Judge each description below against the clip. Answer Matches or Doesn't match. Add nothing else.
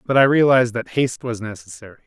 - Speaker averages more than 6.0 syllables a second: Matches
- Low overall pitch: Matches